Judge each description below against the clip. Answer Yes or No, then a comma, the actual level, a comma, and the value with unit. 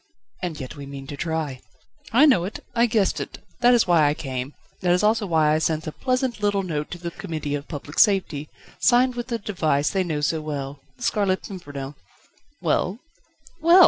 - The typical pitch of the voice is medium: Yes, medium, 170 Hz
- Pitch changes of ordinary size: No, wide, 6.1 semitones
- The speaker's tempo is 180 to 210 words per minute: Yes, average, 200 wpm